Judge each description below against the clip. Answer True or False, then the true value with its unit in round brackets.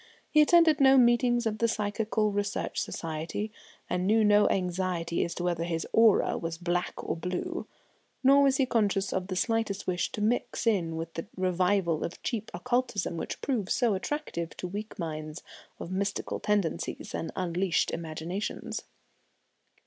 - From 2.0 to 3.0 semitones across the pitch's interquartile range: False (4.7 semitones)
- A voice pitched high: True (195 Hz)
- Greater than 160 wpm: False (155 wpm)